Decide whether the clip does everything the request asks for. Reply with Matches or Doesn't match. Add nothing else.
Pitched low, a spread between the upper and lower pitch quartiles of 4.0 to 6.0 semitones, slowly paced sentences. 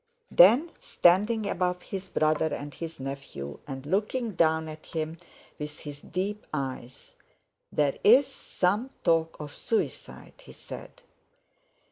Doesn't match